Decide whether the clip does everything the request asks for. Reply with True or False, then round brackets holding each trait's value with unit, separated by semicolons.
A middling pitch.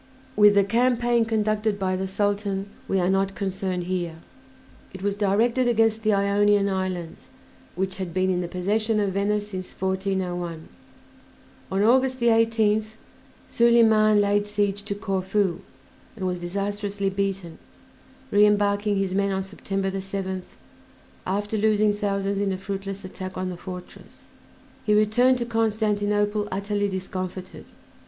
False (200 Hz)